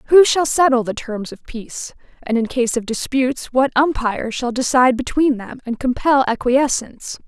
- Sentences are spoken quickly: No, average, 175 wpm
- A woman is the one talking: Yes, female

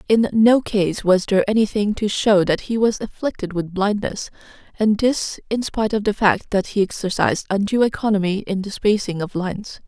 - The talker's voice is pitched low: No, high, 205 Hz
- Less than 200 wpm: Yes, average, 190 wpm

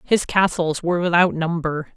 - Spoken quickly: No, average, 155 wpm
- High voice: No, medium, 170 Hz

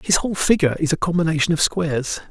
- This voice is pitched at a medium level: Yes, medium, 165 Hz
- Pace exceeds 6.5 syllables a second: Yes, 7.0 syllables/s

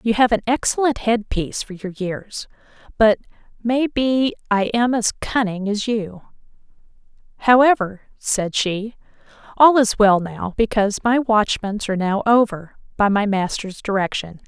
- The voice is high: Yes, high, 215 Hz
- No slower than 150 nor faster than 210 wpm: No, average, 140 wpm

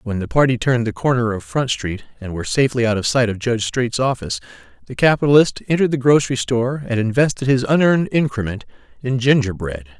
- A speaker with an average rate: Yes, average, 190 wpm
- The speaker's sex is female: No, male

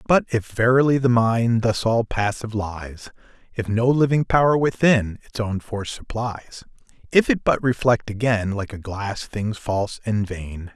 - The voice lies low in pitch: Yes, low, 110 Hz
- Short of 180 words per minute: Yes, average, 165 wpm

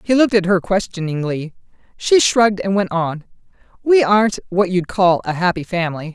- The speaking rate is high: No, average, 175 wpm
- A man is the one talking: No, female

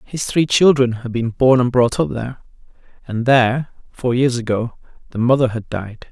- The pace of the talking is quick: No, average, 185 wpm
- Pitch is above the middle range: No, low, 125 Hz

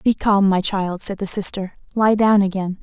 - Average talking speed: No, fast, 210 wpm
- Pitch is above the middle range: Yes, high, 195 Hz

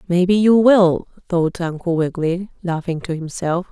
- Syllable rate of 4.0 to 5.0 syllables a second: Yes, 4.7 syllables/s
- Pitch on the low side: No, medium, 175 Hz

